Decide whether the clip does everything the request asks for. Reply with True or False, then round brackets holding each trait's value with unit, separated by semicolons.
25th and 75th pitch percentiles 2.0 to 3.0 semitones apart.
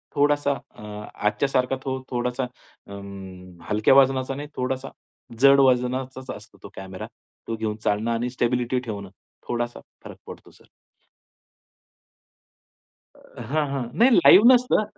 False (3.6 semitones)